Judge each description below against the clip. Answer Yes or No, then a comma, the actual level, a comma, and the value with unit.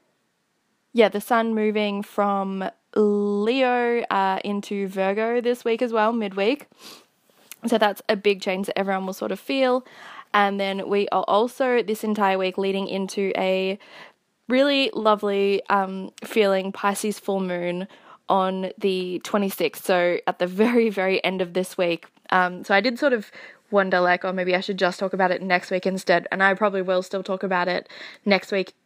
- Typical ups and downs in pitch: No, narrow, 2.3 semitones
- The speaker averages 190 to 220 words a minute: No, average, 175 wpm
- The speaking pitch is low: No, high, 200 Hz